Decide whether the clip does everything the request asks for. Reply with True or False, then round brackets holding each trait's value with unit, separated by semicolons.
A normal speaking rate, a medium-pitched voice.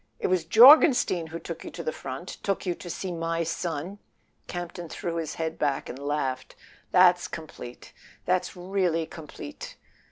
True (155 wpm; 170 Hz)